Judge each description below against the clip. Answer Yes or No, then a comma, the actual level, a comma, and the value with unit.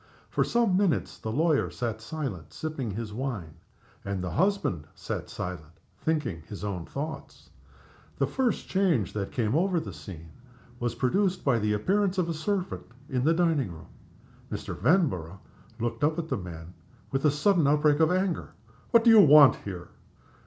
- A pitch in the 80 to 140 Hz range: Yes, low, 135 Hz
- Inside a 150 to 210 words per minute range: Yes, average, 165 wpm